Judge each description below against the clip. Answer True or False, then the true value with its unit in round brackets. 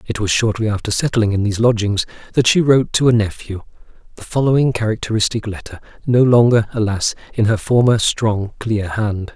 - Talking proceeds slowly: False (175 wpm)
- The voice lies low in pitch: True (110 Hz)